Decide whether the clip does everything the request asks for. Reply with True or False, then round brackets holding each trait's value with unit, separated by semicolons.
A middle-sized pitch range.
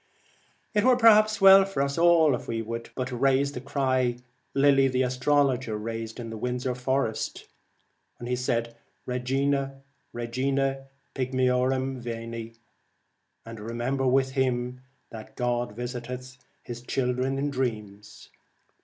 False (2.2 semitones)